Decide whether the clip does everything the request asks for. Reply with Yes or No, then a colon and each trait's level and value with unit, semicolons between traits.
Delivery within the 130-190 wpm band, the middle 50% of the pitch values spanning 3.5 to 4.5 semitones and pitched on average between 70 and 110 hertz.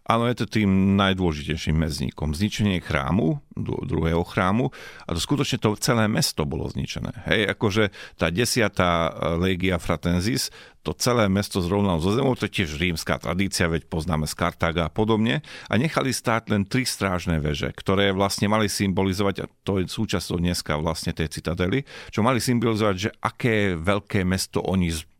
Yes: average, 160 wpm; average, 4.2 semitones; very low, 95 Hz